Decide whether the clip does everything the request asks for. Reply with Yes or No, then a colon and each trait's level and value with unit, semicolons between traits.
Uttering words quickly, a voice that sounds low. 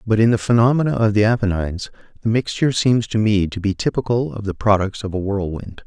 Yes: fast, 215 wpm; low, 105 Hz